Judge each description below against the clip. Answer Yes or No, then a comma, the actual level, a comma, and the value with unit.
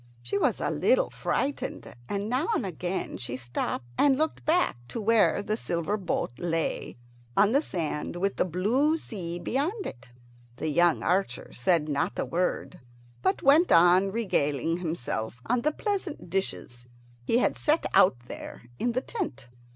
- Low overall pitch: No, high, 190 Hz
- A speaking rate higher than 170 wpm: No, average, 160 wpm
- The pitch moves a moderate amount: No, wide, 7.9 semitones